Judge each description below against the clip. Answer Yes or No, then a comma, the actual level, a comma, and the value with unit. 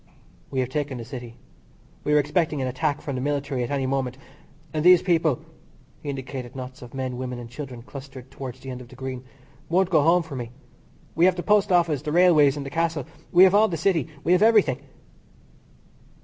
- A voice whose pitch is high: No, medium, 140 Hz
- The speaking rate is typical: No, fast, 215 wpm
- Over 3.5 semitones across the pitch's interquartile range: Yes, average, 4.4 semitones